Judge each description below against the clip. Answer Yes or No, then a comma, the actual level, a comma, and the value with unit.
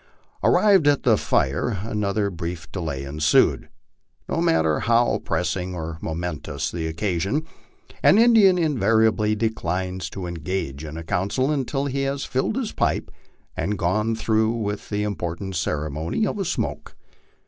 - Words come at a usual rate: Yes, average, 150 wpm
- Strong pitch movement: Yes, wide, 6.2 semitones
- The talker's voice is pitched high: No, low, 100 Hz